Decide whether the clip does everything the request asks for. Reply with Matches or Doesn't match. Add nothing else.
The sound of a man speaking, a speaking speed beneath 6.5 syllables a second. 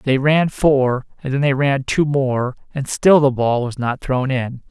Matches